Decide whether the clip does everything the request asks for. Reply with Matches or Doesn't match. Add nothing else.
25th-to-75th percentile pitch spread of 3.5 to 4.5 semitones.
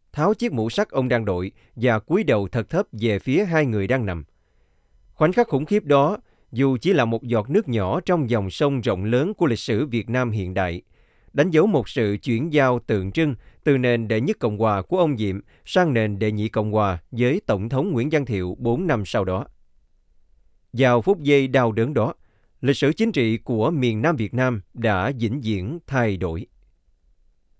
Doesn't match